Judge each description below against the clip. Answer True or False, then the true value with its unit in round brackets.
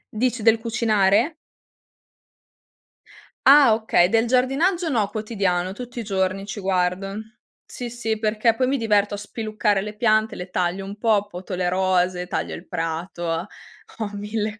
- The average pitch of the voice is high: True (210 Hz)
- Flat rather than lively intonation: False (3.3 semitones)